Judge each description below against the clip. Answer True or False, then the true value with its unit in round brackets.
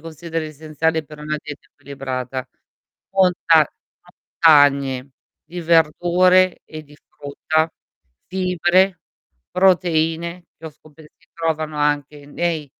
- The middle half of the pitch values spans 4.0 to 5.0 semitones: False (2.7 semitones)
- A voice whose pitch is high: False (160 Hz)